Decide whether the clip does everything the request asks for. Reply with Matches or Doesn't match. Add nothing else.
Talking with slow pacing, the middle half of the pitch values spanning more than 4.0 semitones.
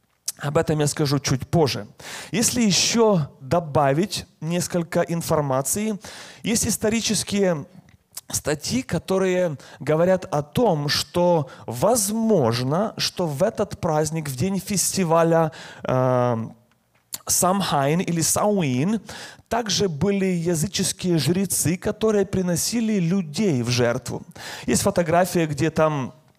Matches